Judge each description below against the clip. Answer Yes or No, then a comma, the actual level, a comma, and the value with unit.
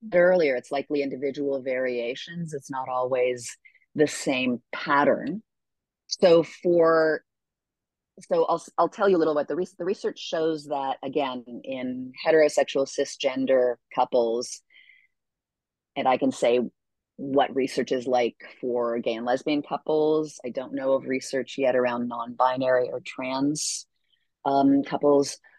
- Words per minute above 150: No, slow, 135 wpm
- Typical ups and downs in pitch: Yes, average, 3.6 semitones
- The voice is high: No, low, 135 Hz